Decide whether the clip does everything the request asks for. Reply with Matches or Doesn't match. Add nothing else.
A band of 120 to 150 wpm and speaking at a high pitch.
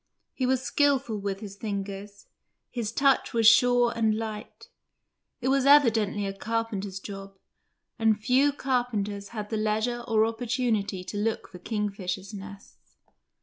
Matches